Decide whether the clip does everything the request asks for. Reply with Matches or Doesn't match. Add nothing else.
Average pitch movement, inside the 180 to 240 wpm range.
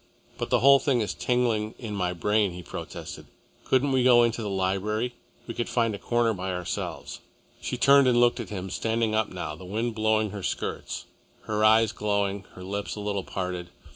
Matches